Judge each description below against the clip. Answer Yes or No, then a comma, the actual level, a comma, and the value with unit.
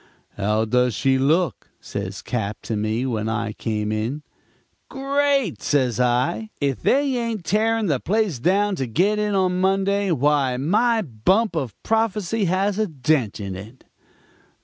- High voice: No, medium, 155 Hz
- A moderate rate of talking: Yes, average, 150 wpm